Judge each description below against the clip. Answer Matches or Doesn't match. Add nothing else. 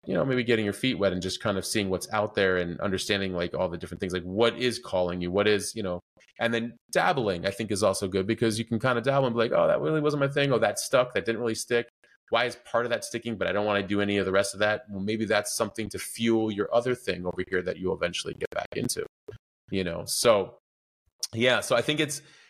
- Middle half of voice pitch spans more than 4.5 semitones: Doesn't match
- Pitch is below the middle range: Matches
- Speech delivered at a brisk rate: Matches